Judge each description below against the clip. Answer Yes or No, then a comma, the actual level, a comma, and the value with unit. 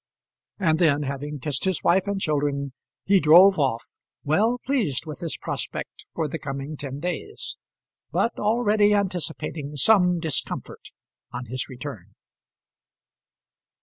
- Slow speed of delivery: Yes, slow, 125 wpm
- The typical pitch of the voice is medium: Yes, medium, 155 Hz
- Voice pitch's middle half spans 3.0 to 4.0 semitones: No, wide, 5.4 semitones